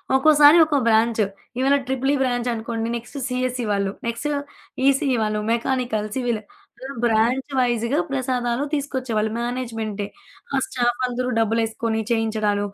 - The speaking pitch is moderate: No, high, 240 Hz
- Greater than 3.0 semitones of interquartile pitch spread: No, narrow, 2.6 semitones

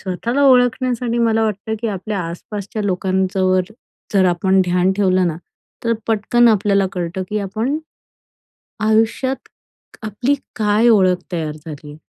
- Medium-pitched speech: No, high, 205 Hz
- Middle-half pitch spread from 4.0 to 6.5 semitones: No, average, 3.6 semitones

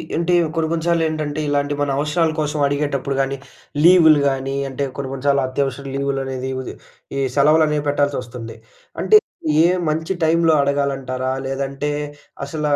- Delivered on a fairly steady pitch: Yes, narrow, 2.3 semitones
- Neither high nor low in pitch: Yes, medium, 145 Hz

